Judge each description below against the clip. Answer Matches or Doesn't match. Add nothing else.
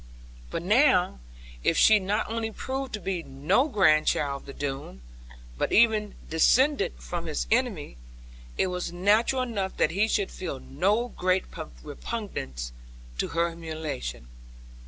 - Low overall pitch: Doesn't match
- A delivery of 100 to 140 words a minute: Matches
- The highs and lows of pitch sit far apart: Matches